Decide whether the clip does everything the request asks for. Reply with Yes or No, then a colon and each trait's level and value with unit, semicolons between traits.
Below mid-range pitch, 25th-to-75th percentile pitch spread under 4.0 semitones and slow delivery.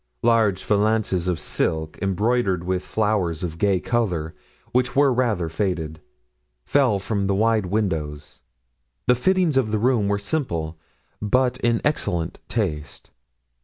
No: low, 100 Hz; average, 5.3 semitones; slow, 130 wpm